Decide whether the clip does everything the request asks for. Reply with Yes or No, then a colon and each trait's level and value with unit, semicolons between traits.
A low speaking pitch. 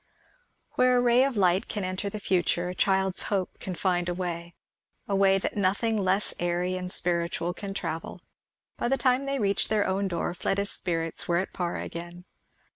No: medium, 185 Hz